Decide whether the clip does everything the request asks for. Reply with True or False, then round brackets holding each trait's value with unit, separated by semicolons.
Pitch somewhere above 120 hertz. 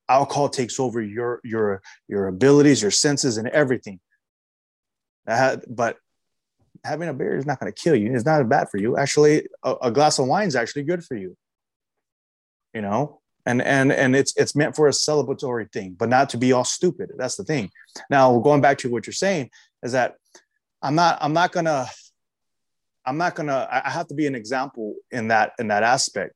True (135 Hz)